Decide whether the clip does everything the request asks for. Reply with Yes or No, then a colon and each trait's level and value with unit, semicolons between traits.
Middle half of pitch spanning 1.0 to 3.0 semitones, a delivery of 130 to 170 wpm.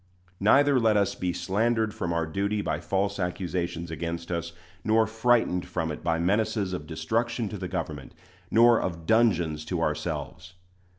No: average, 4.6 semitones; average, 160 wpm